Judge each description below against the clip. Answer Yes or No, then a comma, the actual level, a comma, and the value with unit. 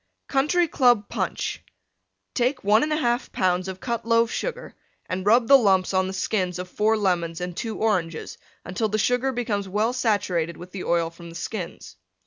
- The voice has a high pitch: Yes, high, 205 Hz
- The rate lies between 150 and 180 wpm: Yes, average, 175 wpm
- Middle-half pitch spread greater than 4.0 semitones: Yes, average, 4.8 semitones